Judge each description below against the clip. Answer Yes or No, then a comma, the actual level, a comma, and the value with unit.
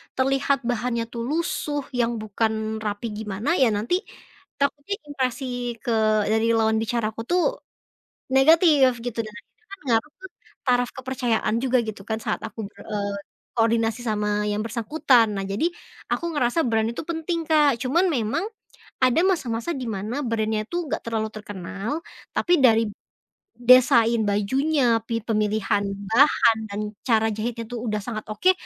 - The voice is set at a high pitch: Yes, high, 235 Hz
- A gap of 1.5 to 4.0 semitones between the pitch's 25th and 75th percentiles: Yes, average, 3.7 semitones